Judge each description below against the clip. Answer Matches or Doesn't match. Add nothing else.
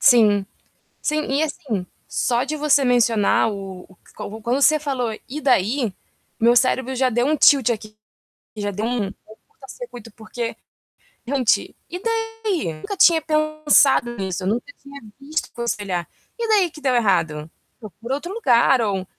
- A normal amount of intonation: Doesn't match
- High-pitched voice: Matches